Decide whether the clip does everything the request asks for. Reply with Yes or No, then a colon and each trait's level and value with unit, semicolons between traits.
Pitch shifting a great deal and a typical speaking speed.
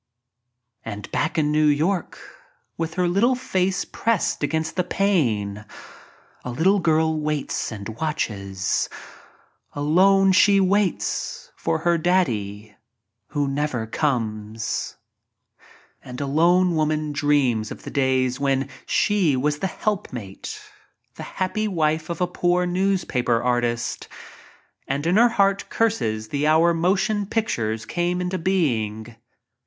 No: wide, 7.0 semitones; slow, 130 wpm